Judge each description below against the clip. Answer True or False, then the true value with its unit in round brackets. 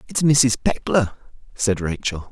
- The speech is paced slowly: True (130 wpm)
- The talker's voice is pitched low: True (115 Hz)